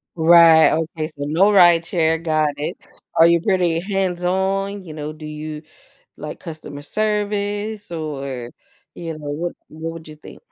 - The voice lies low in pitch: No, medium, 165 Hz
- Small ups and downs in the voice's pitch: No, average, 3.5 semitones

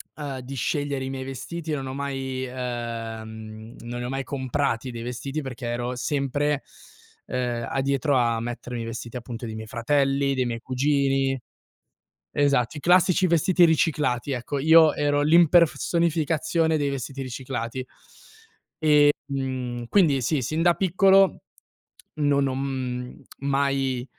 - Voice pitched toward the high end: No, low, 135 Hz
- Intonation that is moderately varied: Yes, average, 3.1 semitones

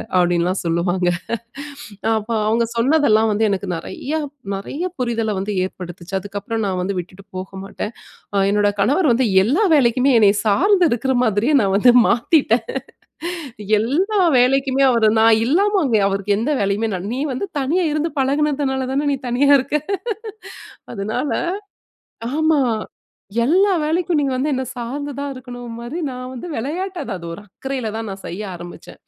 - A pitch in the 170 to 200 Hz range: No, high, 240 Hz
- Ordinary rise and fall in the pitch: No, wide, 5.7 semitones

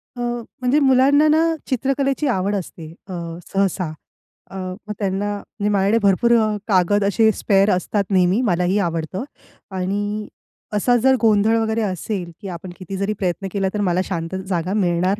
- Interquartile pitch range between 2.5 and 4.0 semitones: Yes, average, 3.2 semitones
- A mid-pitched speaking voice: No, high, 200 Hz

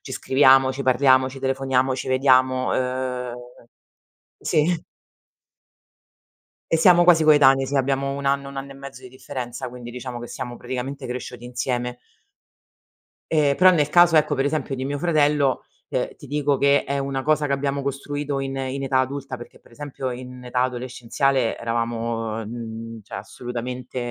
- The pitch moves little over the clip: Yes, narrow, 2.0 semitones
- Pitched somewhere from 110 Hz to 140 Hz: Yes, low, 135 Hz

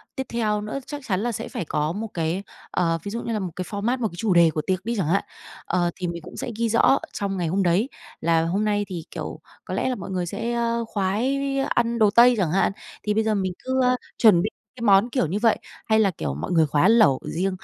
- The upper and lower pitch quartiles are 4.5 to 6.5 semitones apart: Yes, average, 4.8 semitones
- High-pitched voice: Yes, high, 200 Hz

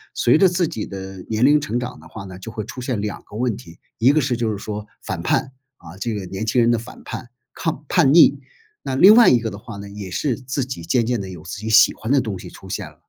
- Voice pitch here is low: Yes, low, 115 Hz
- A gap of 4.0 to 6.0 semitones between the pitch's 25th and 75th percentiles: Yes, average, 4.3 semitones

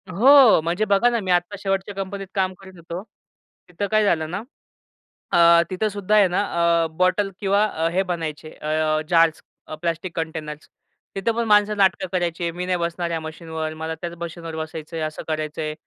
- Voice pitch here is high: No, medium, 175 Hz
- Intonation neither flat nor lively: Yes, average, 3.3 semitones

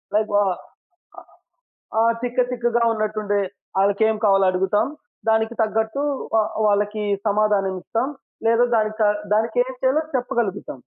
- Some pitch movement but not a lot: No, narrow, 2.3 semitones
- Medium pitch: No, high, 220 Hz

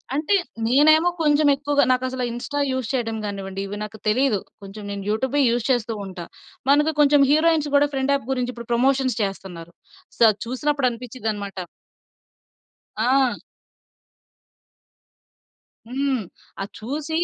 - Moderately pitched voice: No, very high, 255 Hz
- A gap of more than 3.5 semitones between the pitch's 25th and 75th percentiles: Yes, average, 5.0 semitones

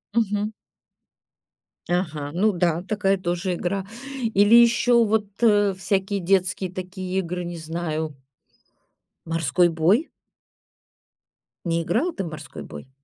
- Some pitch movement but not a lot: Yes, average, 3.3 semitones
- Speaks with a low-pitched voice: No, medium, 185 Hz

